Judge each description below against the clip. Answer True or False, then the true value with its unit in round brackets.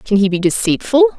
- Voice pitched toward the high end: True (225 Hz)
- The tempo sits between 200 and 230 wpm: True (205 wpm)